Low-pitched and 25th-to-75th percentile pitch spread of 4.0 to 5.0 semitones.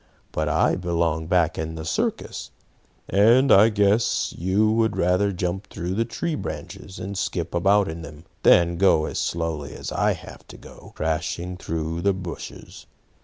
No: very low, 90 Hz; average, 3.4 semitones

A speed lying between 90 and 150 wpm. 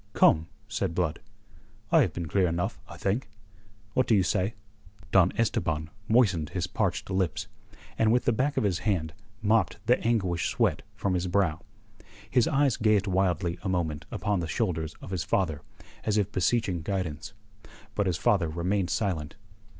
No: average, 165 wpm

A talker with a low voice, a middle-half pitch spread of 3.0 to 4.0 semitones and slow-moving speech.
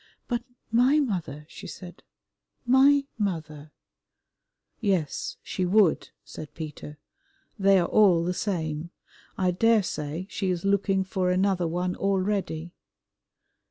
No: medium, 185 Hz; average, 3.3 semitones; slow, 115 wpm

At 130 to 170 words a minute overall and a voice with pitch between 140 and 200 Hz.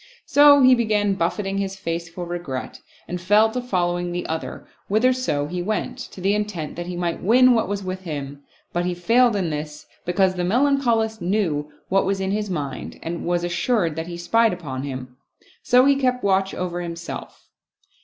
No: average, 195 wpm; medium, 185 Hz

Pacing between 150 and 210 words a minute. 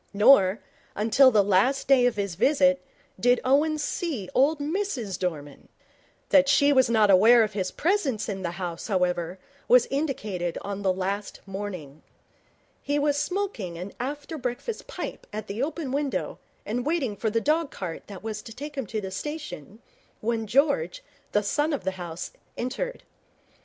Yes: average, 165 wpm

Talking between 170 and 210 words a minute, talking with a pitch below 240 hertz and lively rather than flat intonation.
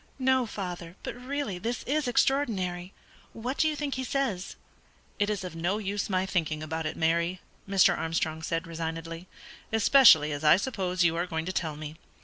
Yes: average, 180 wpm; medium, 185 Hz; wide, 6.1 semitones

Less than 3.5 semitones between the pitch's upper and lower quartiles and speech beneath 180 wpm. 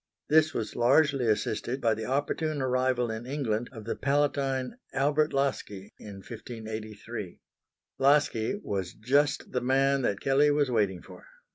No: average, 4.3 semitones; average, 140 wpm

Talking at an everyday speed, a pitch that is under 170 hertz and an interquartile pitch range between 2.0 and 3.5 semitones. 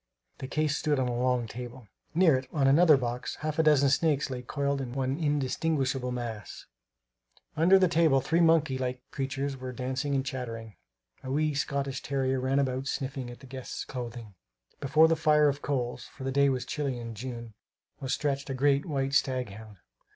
Yes: average, 190 wpm; low, 135 Hz; narrow, 2.4 semitones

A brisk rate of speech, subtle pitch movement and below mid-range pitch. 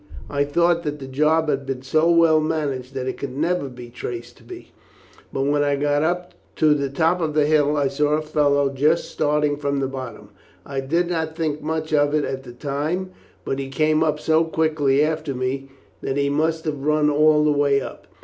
No: fast, 215 wpm; narrow, 2.3 semitones; medium, 150 Hz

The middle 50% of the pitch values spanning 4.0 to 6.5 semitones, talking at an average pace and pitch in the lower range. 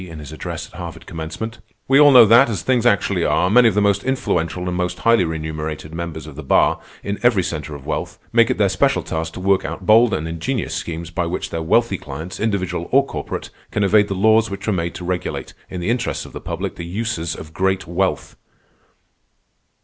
No: average, 5.1 semitones; fast, 220 wpm; very low, 90 Hz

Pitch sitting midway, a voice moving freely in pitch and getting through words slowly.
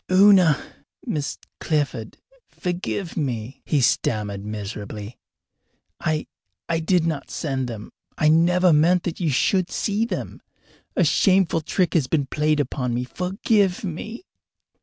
Yes: medium, 155 Hz; wide, 6.1 semitones; slow, 130 wpm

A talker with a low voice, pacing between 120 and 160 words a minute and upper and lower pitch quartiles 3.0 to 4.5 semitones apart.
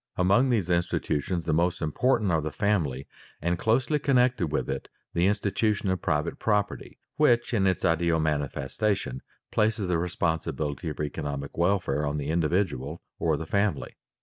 No: very low, 85 Hz; average, 155 wpm; average, 5.1 semitones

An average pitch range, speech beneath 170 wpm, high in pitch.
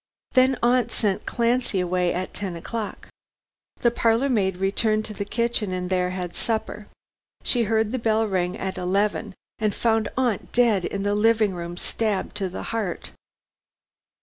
Yes: average, 3.5 semitones; average, 160 wpm; high, 210 Hz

